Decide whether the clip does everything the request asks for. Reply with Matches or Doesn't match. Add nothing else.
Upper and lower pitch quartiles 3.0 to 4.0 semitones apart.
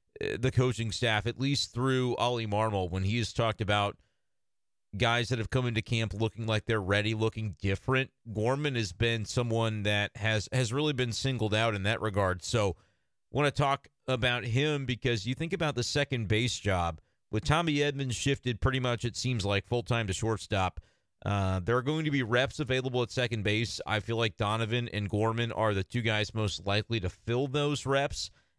Matches